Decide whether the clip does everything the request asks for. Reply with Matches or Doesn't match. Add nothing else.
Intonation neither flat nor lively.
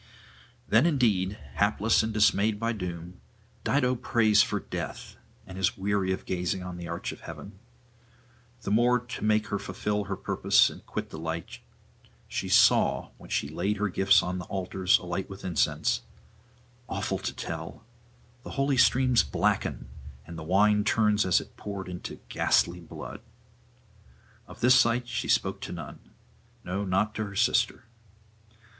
Matches